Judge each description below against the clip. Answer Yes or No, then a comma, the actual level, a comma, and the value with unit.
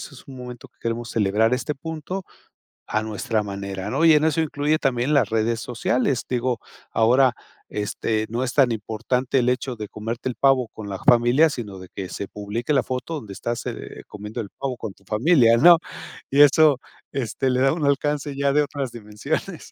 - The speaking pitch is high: No, low, 125 Hz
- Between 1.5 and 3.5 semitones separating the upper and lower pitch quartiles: No, average, 4.1 semitones